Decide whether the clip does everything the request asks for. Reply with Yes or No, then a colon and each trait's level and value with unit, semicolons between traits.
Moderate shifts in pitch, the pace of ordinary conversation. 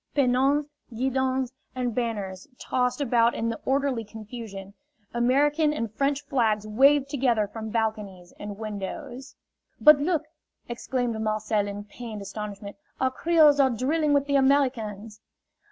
No: average, 4.3 semitones; slow, 130 wpm